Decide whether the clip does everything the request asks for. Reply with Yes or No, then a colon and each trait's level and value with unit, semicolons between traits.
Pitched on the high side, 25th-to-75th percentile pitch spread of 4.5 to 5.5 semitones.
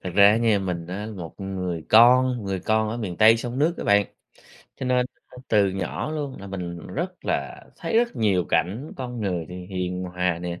No: low, 100 Hz; average, 5.1 semitones